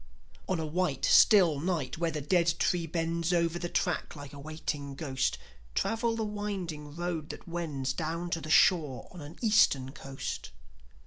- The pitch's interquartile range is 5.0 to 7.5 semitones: No, average, 3.2 semitones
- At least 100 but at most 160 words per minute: No, average, 170 wpm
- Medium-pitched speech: Yes, medium, 165 Hz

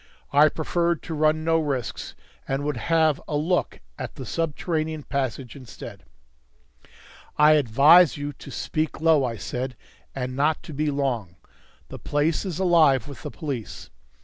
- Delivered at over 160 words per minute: No, average, 150 wpm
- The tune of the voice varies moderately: Yes, average, 3.0 semitones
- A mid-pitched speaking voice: Yes, medium, 150 Hz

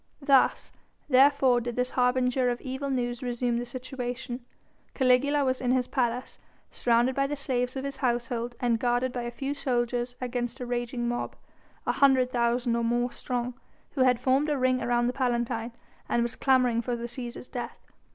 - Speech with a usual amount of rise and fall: No, narrow, 1.3 semitones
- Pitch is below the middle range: No, very high, 250 Hz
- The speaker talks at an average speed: Yes, average, 180 wpm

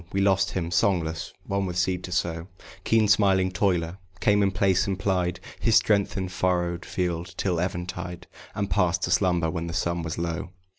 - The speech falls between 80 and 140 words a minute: No, average, 185 wpm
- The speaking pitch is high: No, very low, 90 Hz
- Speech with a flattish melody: Yes, narrow, 2.0 semitones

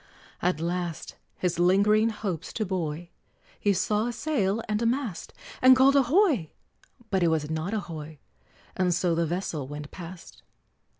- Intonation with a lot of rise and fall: No, average, 4.8 semitones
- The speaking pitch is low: No, medium, 185 Hz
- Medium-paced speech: Yes, average, 160 wpm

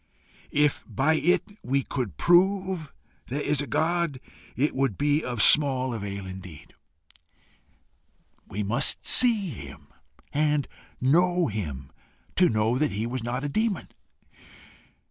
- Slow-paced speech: Yes, slow, 125 wpm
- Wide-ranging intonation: Yes, wide, 6.1 semitones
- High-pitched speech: No, medium, 140 Hz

